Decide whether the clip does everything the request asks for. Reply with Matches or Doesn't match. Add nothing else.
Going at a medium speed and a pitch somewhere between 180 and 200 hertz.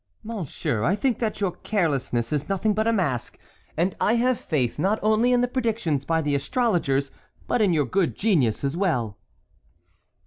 Matches